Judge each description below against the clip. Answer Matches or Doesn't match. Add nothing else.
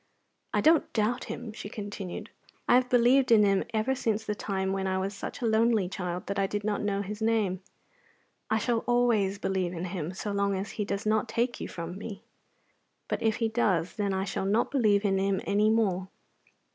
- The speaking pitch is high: Matches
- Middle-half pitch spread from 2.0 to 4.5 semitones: Matches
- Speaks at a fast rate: Matches